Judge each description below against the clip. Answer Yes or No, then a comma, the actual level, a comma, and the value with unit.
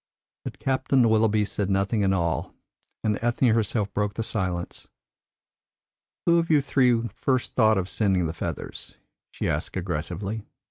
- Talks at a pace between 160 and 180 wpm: No, average, 145 wpm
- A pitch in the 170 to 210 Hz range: No, low, 105 Hz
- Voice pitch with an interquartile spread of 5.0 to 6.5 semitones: No, average, 3.6 semitones